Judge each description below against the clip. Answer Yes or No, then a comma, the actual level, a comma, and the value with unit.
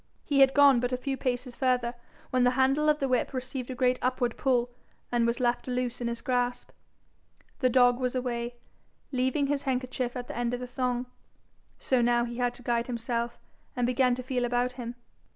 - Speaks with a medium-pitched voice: No, very high, 250 Hz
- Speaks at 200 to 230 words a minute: Yes, fast, 205 wpm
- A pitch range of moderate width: No, narrow, 1.2 semitones